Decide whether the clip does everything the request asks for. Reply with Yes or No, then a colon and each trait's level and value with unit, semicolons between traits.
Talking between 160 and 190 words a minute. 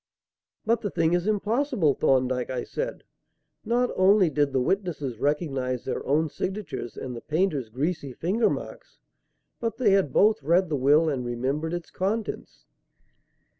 No: average, 150 wpm